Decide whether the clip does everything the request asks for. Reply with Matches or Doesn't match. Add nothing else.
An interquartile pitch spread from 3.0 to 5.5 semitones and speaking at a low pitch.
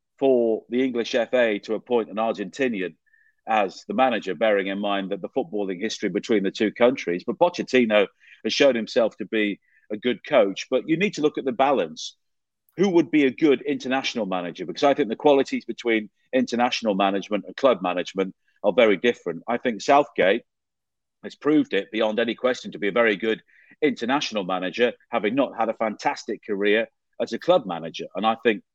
Matches